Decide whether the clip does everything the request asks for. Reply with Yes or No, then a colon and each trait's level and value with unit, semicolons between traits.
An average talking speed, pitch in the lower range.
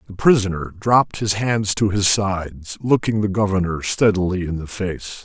Yes: average, 170 wpm; low, 100 Hz